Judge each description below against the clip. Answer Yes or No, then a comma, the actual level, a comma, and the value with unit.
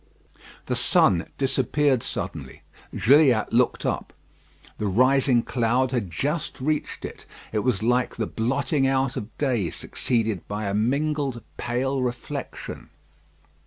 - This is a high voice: No, low, 125 Hz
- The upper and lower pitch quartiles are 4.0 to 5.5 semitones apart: No, average, 3.3 semitones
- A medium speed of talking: No, slow, 125 wpm